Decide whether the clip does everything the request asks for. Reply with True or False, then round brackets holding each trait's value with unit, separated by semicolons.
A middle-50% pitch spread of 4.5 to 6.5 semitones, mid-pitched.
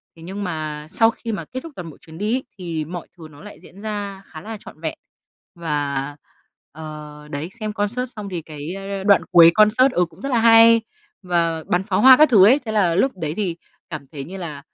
True (5.2 semitones; 180 Hz)